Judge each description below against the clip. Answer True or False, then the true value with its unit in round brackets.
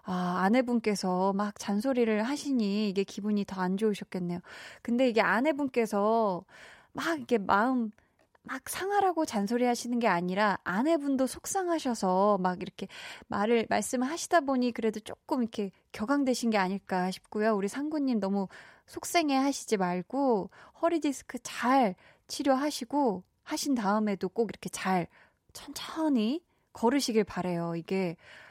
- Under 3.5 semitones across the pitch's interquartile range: False (5.2 semitones)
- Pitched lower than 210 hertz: False (225 Hz)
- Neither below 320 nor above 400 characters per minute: False (310 characters per minute)